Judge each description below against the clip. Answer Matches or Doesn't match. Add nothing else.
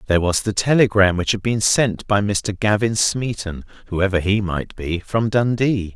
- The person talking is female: Doesn't match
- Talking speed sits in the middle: Matches